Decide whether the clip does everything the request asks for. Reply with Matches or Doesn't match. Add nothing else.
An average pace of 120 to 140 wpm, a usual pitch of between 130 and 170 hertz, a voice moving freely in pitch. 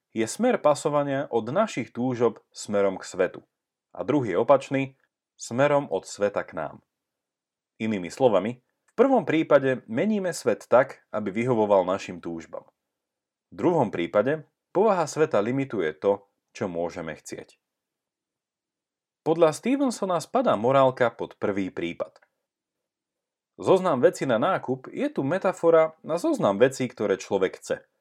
Matches